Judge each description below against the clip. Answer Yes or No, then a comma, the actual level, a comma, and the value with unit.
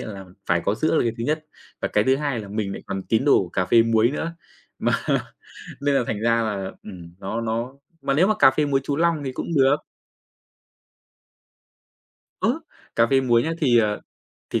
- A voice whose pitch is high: No, low, 115 Hz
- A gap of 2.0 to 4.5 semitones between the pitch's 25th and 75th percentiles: No, average, 4.9 semitones